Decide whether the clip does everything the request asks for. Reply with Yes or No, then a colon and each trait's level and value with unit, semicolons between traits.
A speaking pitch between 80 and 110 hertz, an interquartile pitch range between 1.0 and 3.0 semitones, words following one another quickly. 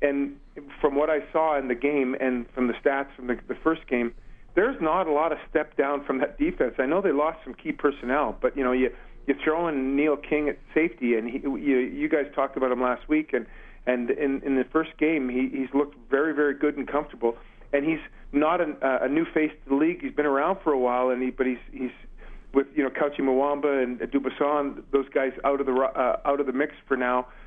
No: medium, 140 Hz; narrow, 2.5 semitones; fast, 240 wpm